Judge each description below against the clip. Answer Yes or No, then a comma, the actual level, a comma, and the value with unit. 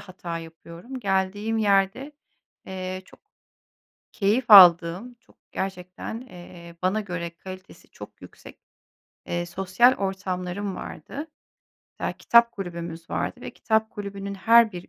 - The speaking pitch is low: No, high, 190 Hz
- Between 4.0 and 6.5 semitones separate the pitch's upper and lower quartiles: No, average, 3.4 semitones